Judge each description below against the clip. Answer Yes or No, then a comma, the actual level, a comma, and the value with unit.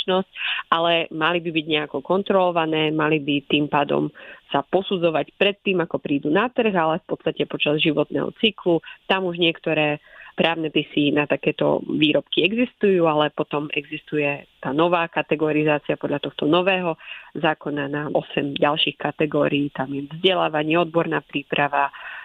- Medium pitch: Yes, medium, 155 Hz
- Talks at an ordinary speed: Yes, average, 140 wpm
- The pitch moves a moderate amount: Yes, average, 3.0 semitones